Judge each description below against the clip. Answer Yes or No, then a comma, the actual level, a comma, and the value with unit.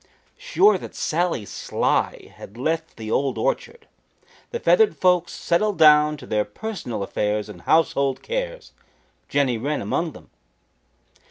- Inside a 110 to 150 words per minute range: Yes, slow, 135 wpm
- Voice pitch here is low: No, medium, 160 Hz